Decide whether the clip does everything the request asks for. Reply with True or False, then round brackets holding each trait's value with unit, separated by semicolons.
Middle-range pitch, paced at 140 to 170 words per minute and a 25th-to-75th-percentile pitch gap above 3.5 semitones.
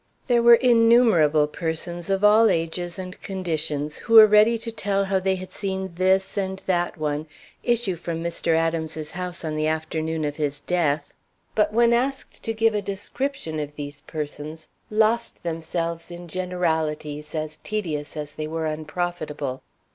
True (170 Hz; 160 wpm; 4.5 semitones)